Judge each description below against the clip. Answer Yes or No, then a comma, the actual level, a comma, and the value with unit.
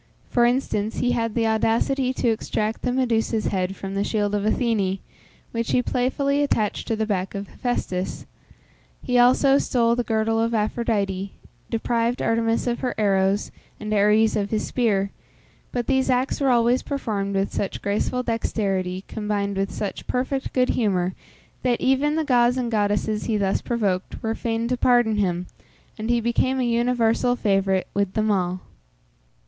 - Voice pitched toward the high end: Yes, high, 225 Hz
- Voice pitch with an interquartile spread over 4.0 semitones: No, average, 3.3 semitones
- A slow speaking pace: No, average, 165 wpm